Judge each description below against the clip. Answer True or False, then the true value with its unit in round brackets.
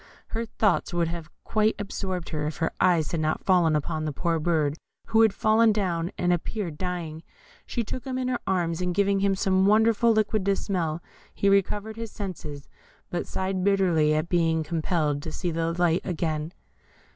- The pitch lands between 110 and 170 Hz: False (180 Hz)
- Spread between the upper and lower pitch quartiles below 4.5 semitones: True (3.7 semitones)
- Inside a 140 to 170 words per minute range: False (185 wpm)